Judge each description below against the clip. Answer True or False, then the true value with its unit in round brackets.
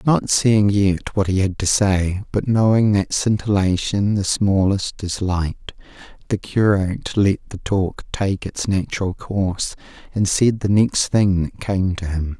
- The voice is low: True (100 Hz)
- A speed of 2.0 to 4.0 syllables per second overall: True (3.9 syllables/s)